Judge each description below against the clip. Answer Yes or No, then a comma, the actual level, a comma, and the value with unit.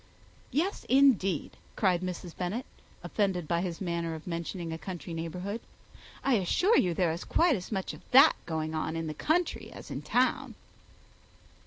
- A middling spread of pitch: Yes, average, 4.5 semitones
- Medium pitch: Yes, medium, 180 Hz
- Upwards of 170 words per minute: No, average, 165 wpm